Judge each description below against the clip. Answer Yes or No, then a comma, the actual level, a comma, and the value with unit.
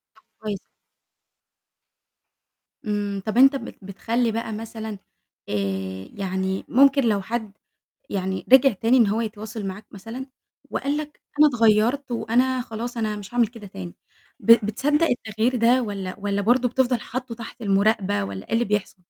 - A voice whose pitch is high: Yes, high, 220 Hz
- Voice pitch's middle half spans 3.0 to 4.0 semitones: Yes, average, 3.5 semitones